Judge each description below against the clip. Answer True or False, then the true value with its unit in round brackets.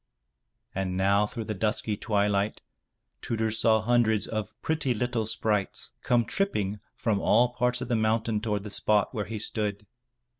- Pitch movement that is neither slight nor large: False (2.1 semitones)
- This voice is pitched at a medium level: False (110 Hz)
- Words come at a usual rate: True (155 wpm)